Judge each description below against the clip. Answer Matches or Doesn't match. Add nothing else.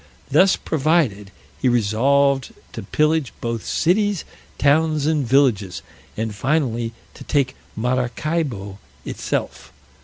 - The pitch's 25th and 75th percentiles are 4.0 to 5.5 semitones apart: Matches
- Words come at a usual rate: Doesn't match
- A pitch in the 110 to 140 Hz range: Matches